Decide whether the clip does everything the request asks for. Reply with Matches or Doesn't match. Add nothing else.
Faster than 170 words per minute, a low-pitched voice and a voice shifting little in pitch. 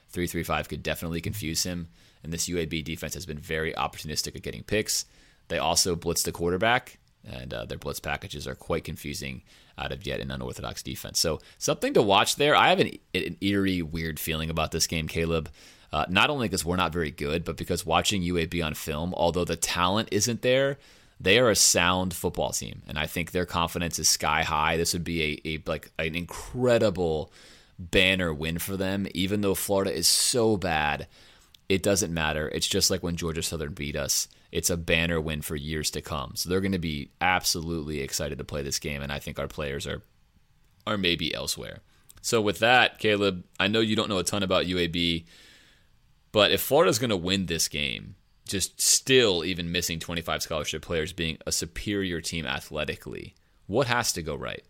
Doesn't match